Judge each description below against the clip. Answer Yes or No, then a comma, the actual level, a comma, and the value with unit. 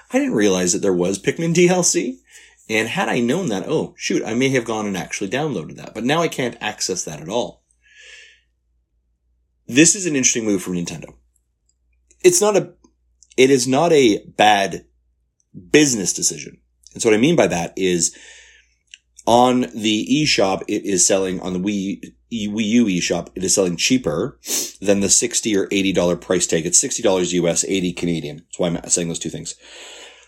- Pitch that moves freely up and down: Yes, wide, 9.0 semitones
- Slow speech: No, average, 180 wpm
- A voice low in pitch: Yes, very low, 95 Hz